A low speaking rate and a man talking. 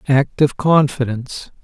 Yes: slow, 110 wpm; male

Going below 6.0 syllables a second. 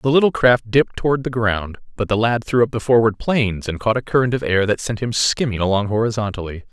No: 6.1 syllables/s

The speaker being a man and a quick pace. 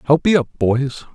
Yes: male; fast, 210 wpm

